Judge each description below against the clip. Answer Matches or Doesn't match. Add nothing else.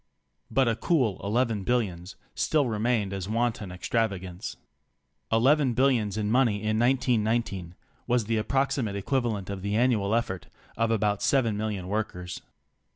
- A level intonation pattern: Doesn't match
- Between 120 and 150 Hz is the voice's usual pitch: Doesn't match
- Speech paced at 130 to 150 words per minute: Matches